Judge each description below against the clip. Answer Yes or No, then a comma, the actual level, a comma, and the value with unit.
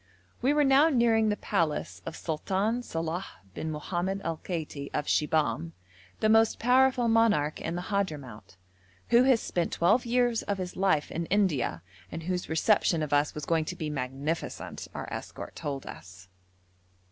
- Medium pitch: Yes, medium, 175 Hz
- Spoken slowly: No, average, 160 wpm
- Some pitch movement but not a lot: No, wide, 6.7 semitones